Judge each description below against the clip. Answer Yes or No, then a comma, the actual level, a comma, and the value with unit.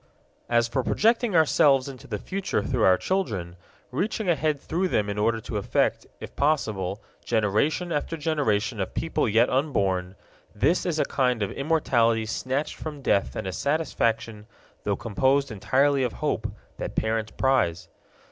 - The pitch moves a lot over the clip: Yes, wide, 6.1 semitones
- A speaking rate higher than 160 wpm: No, average, 155 wpm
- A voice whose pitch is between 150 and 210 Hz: No, low, 130 Hz